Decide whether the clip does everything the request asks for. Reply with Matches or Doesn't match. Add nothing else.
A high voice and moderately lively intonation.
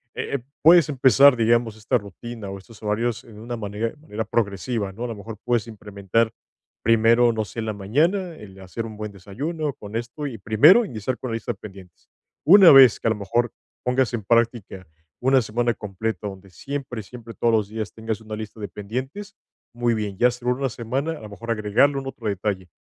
Doesn't match